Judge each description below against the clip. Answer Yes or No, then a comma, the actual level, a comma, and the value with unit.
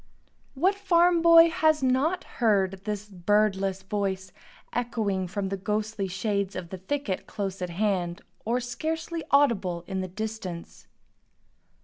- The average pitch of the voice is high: Yes, high, 210 Hz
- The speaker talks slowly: Yes, slow, 130 wpm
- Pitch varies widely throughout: Yes, wide, 5.9 semitones